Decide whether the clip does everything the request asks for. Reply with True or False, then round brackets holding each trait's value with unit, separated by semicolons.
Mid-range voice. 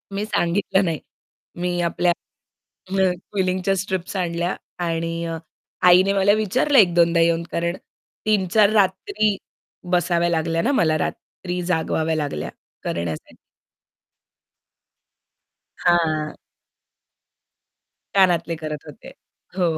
True (175 Hz)